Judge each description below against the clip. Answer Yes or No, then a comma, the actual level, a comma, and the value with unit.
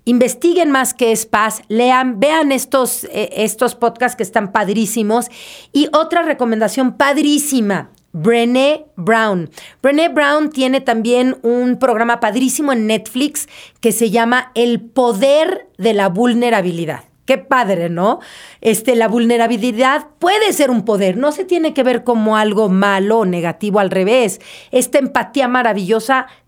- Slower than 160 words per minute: Yes, average, 140 wpm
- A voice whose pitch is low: No, high, 240 Hz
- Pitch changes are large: No, average, 3.4 semitones